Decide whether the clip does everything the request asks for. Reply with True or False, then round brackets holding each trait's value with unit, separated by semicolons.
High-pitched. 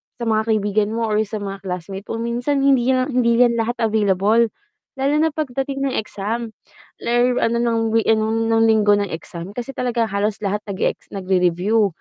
True (225 Hz)